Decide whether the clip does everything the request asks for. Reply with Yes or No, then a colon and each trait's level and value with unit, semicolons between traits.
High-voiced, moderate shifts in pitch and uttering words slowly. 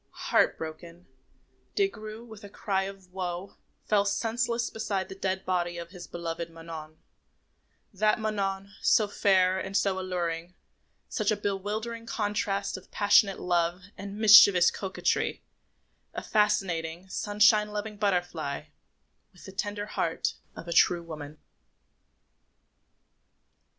Yes: high, 195 Hz; average, 3.1 semitones; slow, 125 wpm